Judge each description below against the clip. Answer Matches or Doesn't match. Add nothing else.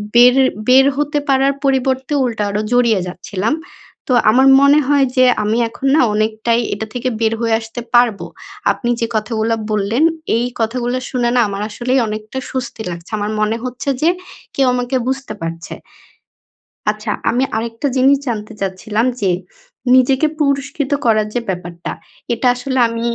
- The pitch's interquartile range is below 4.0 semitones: Matches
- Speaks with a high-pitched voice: Matches